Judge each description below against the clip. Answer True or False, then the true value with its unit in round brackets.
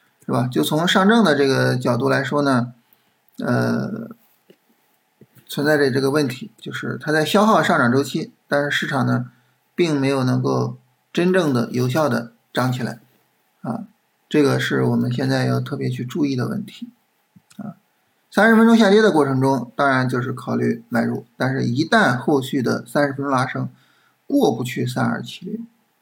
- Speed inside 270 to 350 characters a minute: False (245 characters per minute)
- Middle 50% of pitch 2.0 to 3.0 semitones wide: False (4.6 semitones)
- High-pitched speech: False (135 Hz)